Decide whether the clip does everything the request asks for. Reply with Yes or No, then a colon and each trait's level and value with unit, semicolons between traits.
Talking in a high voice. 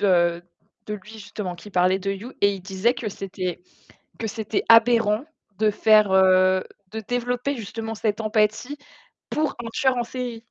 Yes: high, 215 Hz